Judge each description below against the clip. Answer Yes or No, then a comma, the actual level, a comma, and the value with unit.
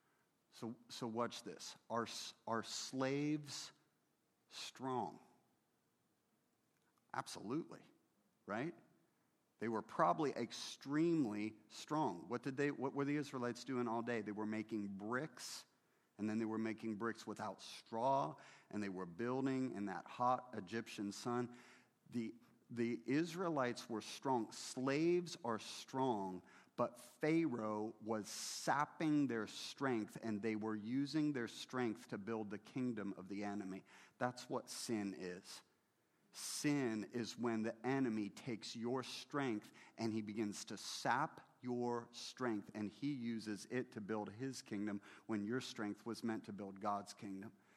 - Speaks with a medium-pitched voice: No, low, 115 Hz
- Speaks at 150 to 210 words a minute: No, slow, 135 wpm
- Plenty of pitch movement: No, average, 3.5 semitones